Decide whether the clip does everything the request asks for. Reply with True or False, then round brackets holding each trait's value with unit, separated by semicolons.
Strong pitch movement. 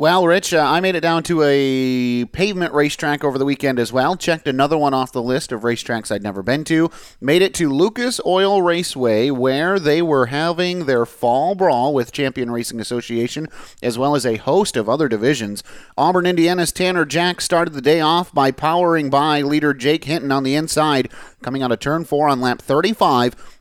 False (4.7 semitones)